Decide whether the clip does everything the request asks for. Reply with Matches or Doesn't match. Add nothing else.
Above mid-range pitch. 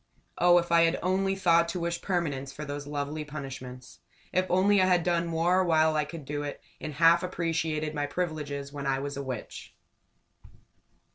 Doesn't match